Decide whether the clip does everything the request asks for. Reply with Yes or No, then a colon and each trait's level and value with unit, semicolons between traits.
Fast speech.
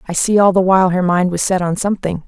Yes: fast, 290 wpm